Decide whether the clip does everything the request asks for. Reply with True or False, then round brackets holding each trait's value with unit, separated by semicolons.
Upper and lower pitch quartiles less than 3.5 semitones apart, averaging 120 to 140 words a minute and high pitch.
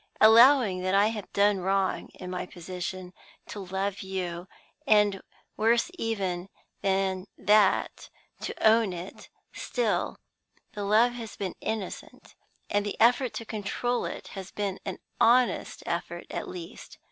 True (2.9 semitones; 135 wpm; 200 Hz)